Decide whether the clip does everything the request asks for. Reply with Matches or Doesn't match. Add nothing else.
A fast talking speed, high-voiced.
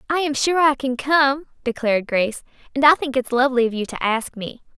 Matches